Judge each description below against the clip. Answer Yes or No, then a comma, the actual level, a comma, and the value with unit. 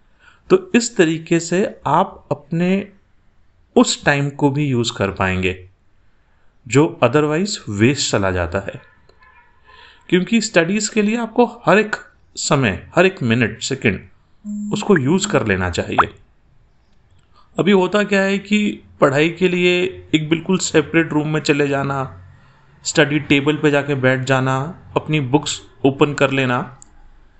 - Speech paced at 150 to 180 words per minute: No, slow, 135 wpm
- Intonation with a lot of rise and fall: Yes, wide, 7.3 semitones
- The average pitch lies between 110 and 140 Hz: No, medium, 150 Hz